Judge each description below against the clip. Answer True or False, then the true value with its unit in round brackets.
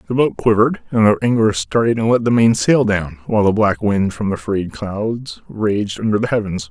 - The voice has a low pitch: True (105 Hz)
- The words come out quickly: True (225 wpm)